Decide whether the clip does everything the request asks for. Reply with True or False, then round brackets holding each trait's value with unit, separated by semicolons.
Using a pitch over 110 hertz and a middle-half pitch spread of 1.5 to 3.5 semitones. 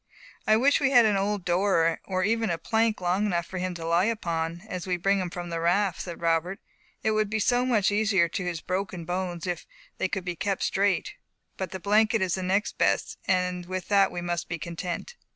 True (185 Hz; 3.1 semitones)